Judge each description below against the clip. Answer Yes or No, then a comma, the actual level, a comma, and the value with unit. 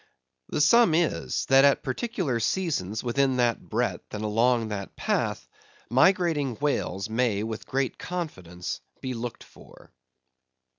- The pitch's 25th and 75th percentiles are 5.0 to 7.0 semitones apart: Yes, average, 5.3 semitones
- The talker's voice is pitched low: Yes, low, 125 Hz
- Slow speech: Yes, slow, 130 wpm